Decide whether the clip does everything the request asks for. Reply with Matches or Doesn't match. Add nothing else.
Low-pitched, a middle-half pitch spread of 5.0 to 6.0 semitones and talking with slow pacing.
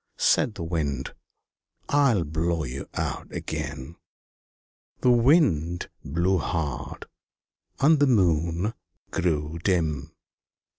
Matches